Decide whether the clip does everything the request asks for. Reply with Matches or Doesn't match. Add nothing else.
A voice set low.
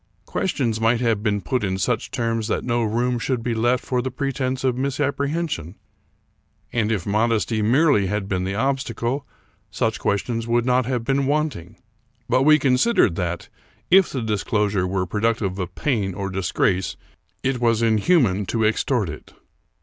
Matches